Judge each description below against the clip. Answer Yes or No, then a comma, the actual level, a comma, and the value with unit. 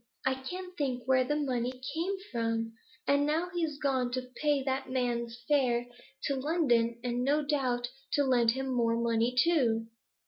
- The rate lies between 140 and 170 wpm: Yes, average, 165 wpm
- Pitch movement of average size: Yes, average, 3.4 semitones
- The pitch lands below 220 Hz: No, very high, 260 Hz